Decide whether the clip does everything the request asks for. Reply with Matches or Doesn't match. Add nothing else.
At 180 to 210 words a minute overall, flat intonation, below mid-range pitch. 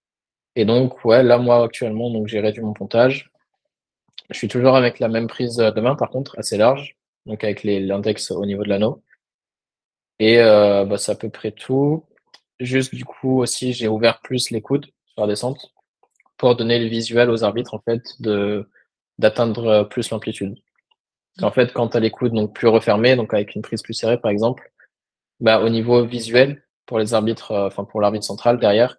Matches